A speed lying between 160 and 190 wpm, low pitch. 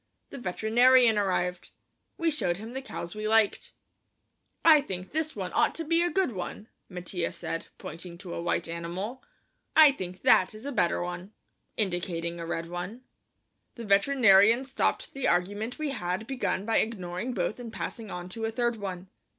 No: average, 180 wpm; high, 205 Hz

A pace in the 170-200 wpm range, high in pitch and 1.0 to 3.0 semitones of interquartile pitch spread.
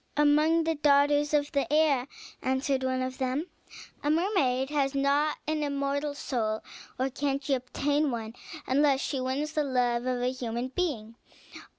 No: average, 160 wpm; very high, 275 Hz; narrow, 2.4 semitones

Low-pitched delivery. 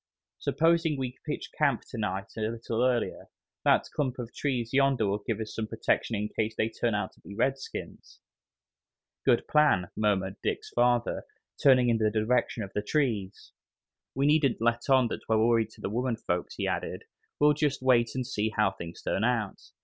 Yes: low, 115 Hz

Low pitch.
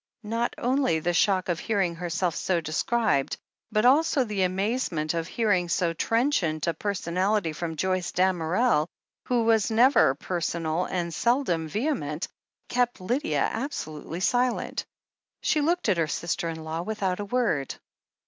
No: medium, 185 Hz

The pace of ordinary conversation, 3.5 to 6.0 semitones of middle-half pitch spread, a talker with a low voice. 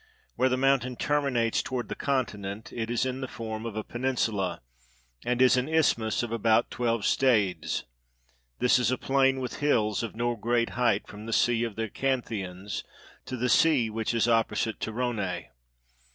No: average, 180 wpm; narrow, 2.6 semitones; low, 120 Hz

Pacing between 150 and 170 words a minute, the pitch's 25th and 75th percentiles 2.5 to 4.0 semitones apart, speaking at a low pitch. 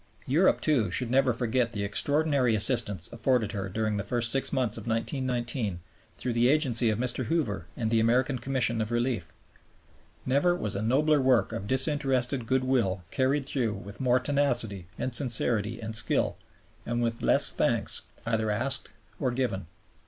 Yes: average, 160 wpm; average, 3.1 semitones; low, 120 Hz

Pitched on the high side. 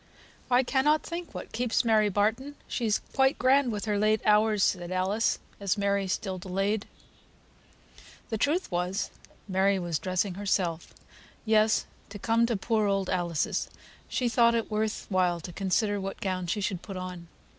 Yes: high, 205 Hz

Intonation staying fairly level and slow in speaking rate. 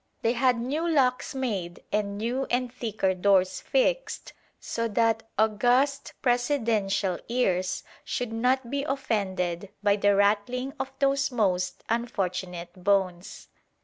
No: average, 4.5 semitones; slow, 120 wpm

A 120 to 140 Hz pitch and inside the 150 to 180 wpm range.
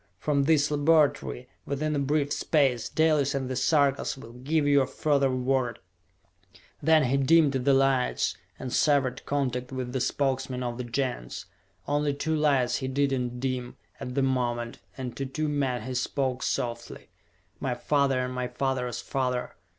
Yes: low, 135 Hz; average, 160 wpm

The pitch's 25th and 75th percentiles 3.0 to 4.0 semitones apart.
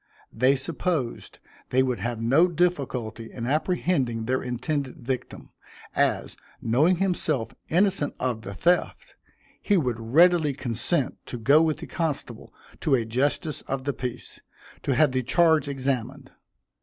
No: average, 4.6 semitones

